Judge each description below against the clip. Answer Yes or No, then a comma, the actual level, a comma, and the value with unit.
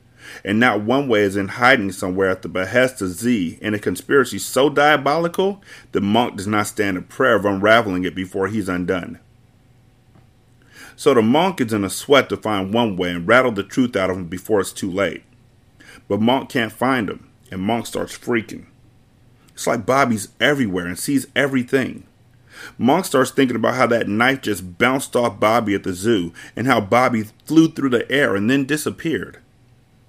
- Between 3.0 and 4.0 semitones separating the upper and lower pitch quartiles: No, average, 4.5 semitones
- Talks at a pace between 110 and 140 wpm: No, average, 185 wpm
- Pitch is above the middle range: No, low, 115 Hz